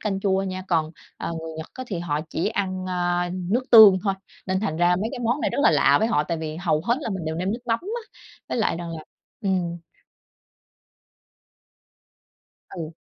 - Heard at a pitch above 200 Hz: No, medium, 185 Hz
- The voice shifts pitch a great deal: No, average, 4.3 semitones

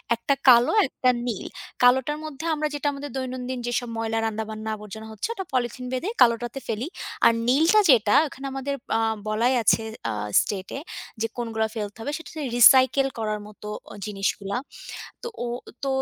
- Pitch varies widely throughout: No, average, 3.8 semitones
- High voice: Yes, high, 245 Hz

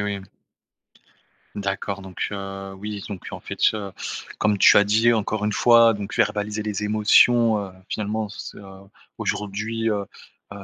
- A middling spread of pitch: No, narrow, 1.4 semitones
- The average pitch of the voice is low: Yes, low, 105 Hz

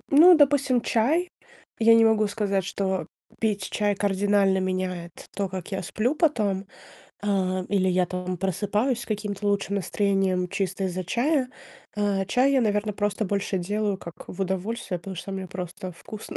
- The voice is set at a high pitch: Yes, high, 200 Hz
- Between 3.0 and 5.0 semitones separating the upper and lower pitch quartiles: No, narrow, 2.6 semitones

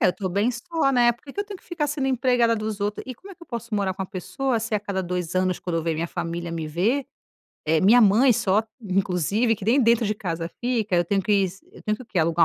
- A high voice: Yes, high, 210 Hz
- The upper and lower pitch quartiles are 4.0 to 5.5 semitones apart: Yes, average, 5.0 semitones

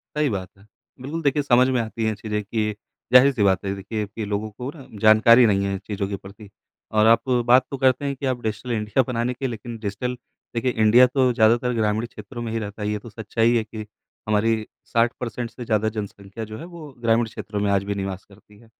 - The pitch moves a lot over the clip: No, average, 2.9 semitones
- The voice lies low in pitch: Yes, low, 110 Hz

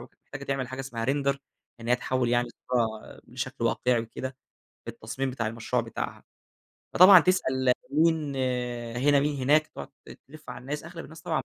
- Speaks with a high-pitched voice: No, low, 135 Hz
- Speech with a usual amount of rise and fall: Yes, average, 3.3 semitones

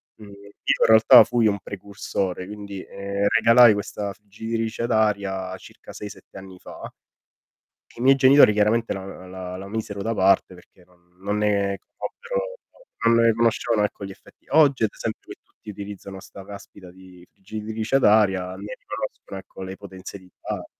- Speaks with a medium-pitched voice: No, low, 100 Hz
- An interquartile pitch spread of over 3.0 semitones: No, narrow, 2.5 semitones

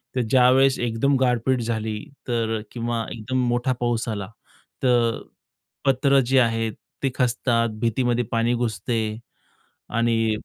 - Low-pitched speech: Yes, low, 120 Hz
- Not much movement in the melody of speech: Yes, narrow, 1.8 semitones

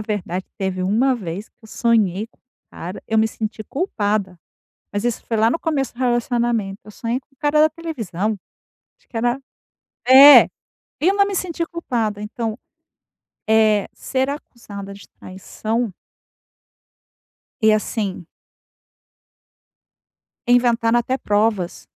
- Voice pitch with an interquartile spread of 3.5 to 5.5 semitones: Yes, average, 3.8 semitones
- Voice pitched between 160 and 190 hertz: No, high, 225 Hz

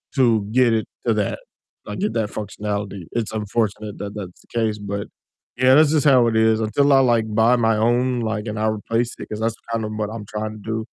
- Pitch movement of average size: No, narrow, 1.9 semitones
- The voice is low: Yes, low, 110 Hz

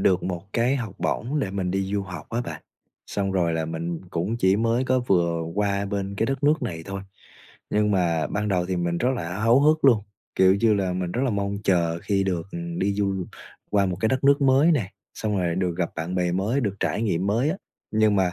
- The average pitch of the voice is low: Yes, low, 100 Hz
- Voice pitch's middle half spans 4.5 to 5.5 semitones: No, average, 4.1 semitones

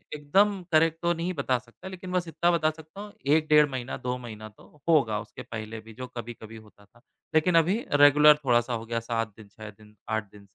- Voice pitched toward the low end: Yes, low, 130 Hz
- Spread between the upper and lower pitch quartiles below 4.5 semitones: No, wide, 6.5 semitones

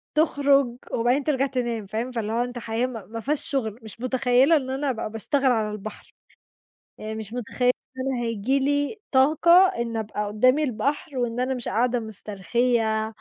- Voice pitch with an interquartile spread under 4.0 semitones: Yes, average, 3.4 semitones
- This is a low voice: No, high, 245 Hz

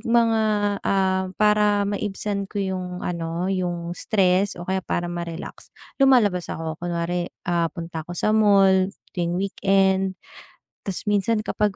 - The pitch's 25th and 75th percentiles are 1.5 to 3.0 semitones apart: Yes, narrow, 2.6 semitones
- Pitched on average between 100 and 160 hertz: No, high, 190 Hz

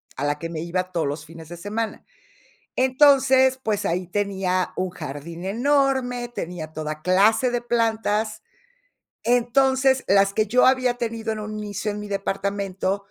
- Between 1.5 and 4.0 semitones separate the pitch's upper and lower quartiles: No, average, 4.9 semitones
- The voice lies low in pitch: No, high, 205 Hz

